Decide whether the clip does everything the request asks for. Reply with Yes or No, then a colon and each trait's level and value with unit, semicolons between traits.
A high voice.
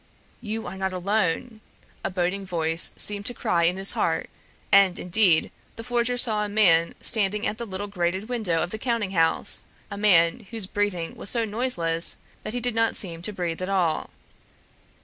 Yes: high, 200 Hz